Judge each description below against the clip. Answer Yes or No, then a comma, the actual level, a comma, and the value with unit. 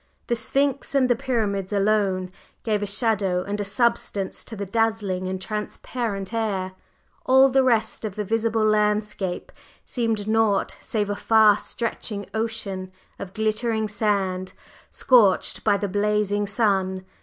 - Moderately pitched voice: No, high, 210 Hz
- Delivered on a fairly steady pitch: Yes, narrow, 2.3 semitones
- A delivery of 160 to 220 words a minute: No, average, 140 wpm